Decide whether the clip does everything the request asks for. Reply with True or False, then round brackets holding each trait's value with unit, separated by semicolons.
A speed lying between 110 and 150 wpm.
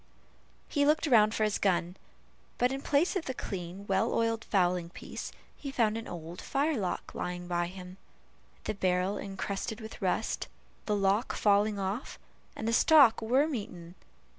False (160 wpm)